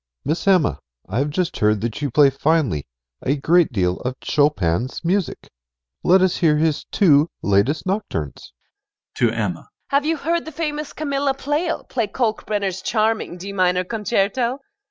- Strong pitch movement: Yes, wide, 8.0 semitones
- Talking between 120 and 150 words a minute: No, average, 160 wpm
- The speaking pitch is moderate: Yes, medium, 180 Hz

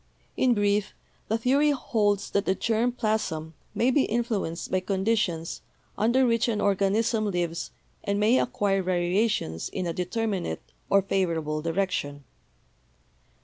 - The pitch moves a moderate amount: Yes, average, 4.1 semitones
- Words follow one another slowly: Yes, slow, 130 wpm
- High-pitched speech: Yes, high, 200 Hz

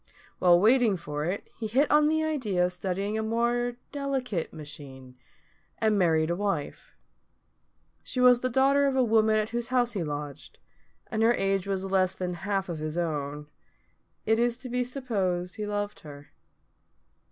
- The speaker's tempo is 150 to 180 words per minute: Yes, average, 170 wpm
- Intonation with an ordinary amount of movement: No, wide, 5.8 semitones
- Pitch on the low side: No, high, 205 Hz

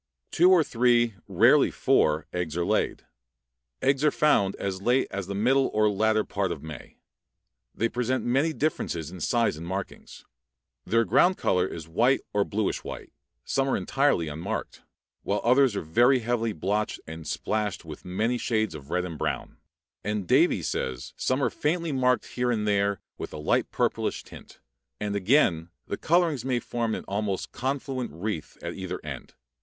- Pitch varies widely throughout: Yes, wide, 5.7 semitones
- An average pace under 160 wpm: No, average, 170 wpm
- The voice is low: Yes, low, 110 Hz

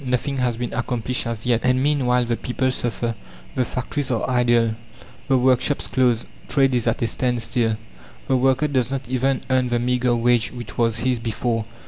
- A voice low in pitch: Yes, low, 125 Hz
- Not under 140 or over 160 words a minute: No, average, 180 wpm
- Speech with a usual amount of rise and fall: No, narrow, 1.6 semitones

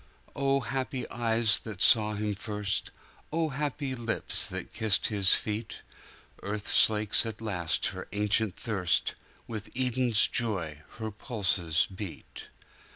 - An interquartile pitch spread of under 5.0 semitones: Yes, average, 2.8 semitones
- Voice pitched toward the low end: Yes, low, 110 Hz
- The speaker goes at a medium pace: No, slow, 120 wpm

